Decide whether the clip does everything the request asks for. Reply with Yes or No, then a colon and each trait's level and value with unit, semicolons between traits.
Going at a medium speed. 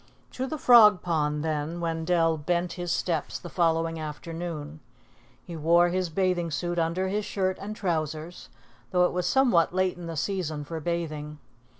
Yes: average, 165 wpm